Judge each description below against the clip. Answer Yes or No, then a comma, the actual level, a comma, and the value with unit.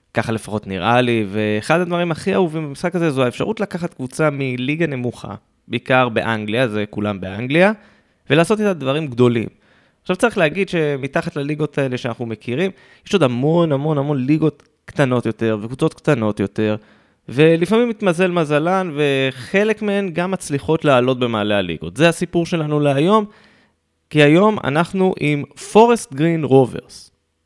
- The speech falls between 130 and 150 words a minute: Yes, average, 140 wpm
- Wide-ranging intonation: Yes, wide, 6.4 semitones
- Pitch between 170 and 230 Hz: No, medium, 145 Hz